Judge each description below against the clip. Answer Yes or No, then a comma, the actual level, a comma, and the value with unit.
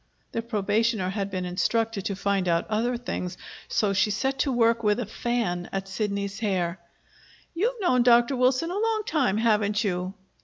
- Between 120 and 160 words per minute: No, average, 175 wpm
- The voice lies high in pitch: Yes, high, 215 Hz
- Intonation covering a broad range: No, average, 3.9 semitones